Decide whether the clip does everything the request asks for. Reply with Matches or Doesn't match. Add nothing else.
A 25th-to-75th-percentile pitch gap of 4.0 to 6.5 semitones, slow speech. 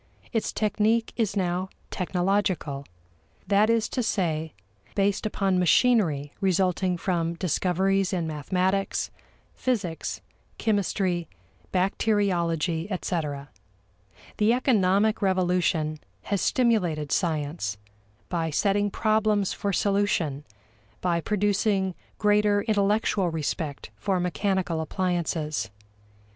Doesn't match